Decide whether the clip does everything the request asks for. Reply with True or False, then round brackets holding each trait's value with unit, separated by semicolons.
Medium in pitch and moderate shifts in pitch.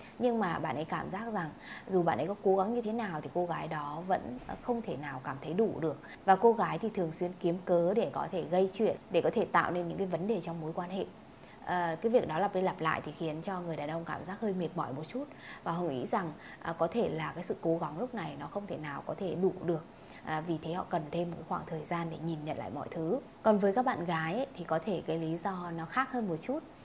True (175 Hz; 3.7 semitones)